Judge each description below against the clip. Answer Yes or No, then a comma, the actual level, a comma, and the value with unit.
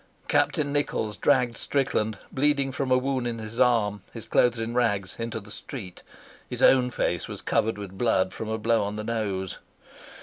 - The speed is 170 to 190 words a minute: Yes, average, 180 wpm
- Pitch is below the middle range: Yes, low, 115 Hz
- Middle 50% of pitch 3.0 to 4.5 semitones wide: Yes, average, 3.4 semitones